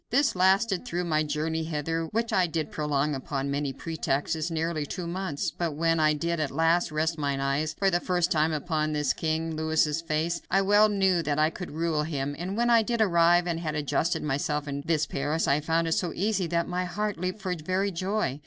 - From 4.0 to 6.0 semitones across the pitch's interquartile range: No, average, 3.0 semitones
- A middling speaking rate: No, fast, 215 wpm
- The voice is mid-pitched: Yes, medium, 165 Hz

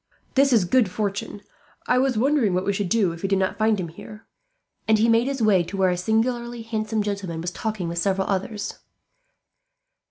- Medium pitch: No, high, 210 Hz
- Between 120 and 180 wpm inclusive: No, average, 200 wpm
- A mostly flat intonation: No, average, 3.3 semitones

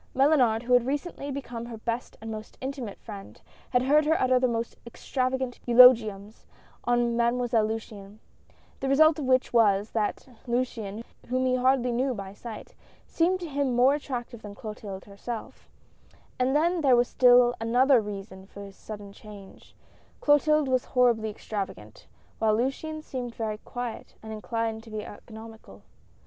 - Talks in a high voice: Yes, high, 240 Hz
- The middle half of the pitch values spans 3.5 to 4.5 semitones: No, average, 3.1 semitones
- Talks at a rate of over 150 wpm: Yes, average, 160 wpm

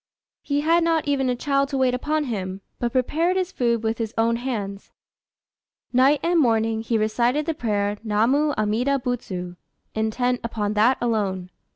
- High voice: Yes, high, 240 Hz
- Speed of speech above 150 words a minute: Yes, average, 165 wpm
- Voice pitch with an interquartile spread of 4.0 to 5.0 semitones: Yes, average, 4.4 semitones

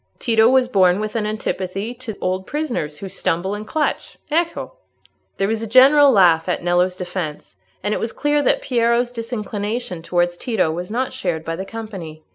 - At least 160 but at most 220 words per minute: Yes, average, 180 wpm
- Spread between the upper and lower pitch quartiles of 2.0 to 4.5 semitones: No, average, 5.0 semitones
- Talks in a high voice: Yes, high, 210 Hz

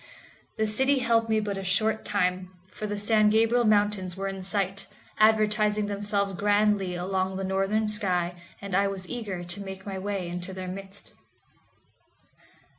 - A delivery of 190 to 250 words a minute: No, average, 160 wpm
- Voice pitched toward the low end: No, high, 200 Hz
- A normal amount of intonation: No, narrow, 2.0 semitones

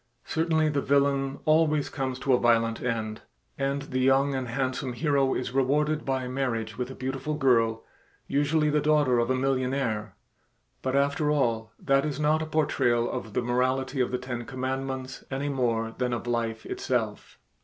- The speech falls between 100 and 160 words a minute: No, average, 170 wpm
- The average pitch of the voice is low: Yes, low, 130 Hz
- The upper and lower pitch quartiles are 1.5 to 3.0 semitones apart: Yes, narrow, 2.6 semitones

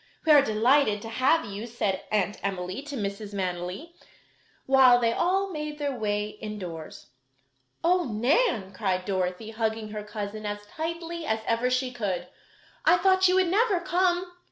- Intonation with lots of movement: Yes, wide, 7.5 semitones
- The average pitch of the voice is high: Yes, high, 225 Hz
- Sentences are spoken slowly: No, average, 155 wpm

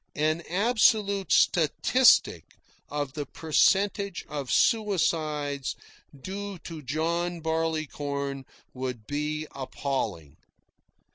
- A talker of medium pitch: Yes, medium, 155 Hz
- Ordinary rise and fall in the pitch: Yes, average, 4.8 semitones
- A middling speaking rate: No, slow, 80 wpm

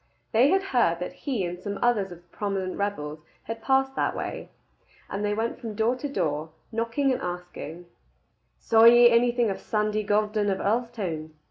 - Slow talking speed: No, average, 175 wpm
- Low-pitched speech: No, high, 215 Hz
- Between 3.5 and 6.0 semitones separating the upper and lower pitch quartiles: Yes, average, 4.5 semitones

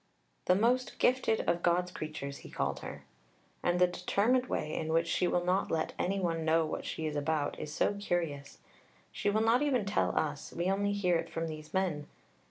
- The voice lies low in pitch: No, medium, 175 Hz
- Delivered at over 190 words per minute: Yes, average, 200 wpm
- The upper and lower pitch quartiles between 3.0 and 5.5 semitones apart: Yes, average, 4.2 semitones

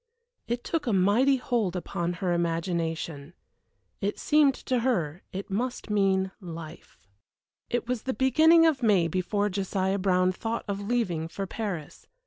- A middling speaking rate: Yes, average, 145 wpm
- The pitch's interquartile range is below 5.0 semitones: No, wide, 5.5 semitones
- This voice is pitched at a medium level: No, high, 195 Hz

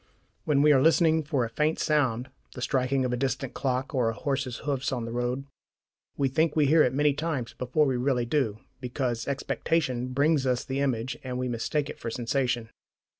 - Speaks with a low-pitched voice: Yes, low, 130 Hz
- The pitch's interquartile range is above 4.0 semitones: No, average, 2.8 semitones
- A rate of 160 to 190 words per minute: No, average, 200 wpm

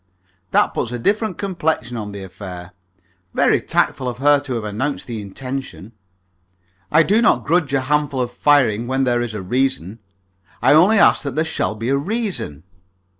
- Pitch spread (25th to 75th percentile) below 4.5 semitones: No, average, 4.8 semitones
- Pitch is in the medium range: No, low, 130 Hz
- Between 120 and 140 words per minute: No, average, 175 wpm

